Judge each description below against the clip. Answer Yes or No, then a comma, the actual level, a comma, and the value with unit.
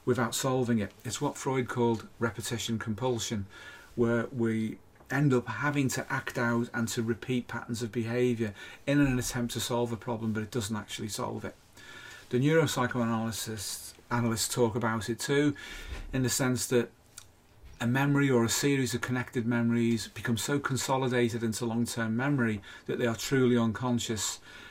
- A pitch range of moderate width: No, narrow, 1.7 semitones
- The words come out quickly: No, average, 165 wpm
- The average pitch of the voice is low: Yes, low, 120 Hz